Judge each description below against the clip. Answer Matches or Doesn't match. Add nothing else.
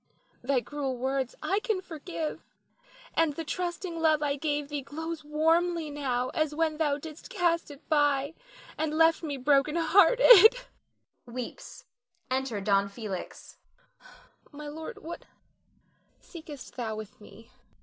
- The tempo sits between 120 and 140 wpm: Matches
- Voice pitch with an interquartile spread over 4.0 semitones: Doesn't match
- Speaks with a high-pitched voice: Matches